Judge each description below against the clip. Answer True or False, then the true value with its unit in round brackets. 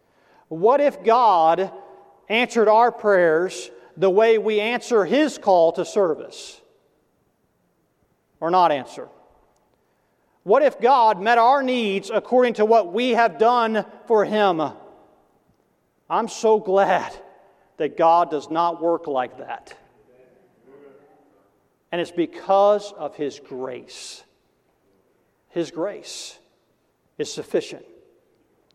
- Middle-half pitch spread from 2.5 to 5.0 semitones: False (5.6 semitones)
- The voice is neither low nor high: False (210 Hz)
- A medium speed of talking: False (105 wpm)